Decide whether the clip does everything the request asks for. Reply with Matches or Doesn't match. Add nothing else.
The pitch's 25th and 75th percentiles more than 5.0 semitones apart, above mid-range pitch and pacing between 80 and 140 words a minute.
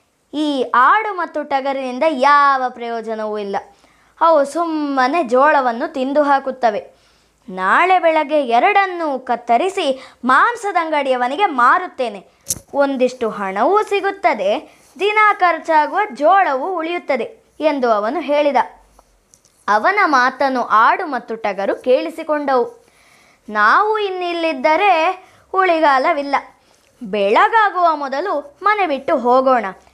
Matches